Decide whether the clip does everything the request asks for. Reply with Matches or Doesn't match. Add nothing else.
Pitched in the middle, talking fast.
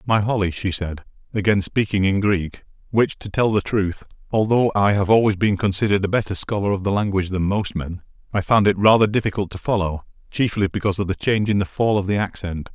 Doesn't match